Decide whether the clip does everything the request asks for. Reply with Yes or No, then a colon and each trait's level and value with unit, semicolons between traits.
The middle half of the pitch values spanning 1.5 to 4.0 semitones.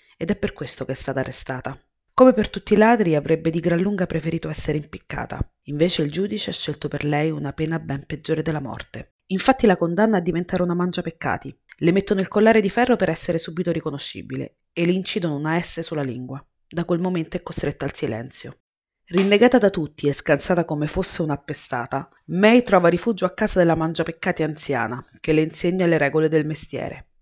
Yes: average, 3.7 semitones